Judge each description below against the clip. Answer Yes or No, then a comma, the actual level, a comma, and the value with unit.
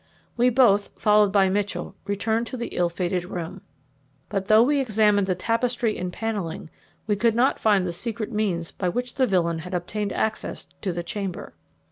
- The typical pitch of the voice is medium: No, high, 205 Hz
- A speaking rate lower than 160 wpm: No, average, 180 wpm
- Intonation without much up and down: No, average, 3.7 semitones